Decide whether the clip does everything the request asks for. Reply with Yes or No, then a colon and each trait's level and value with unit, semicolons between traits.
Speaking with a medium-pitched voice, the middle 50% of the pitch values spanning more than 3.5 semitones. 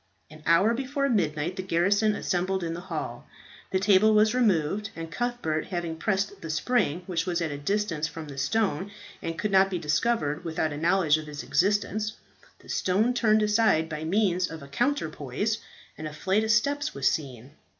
Yes: medium, 180 Hz; average, 5.2 semitones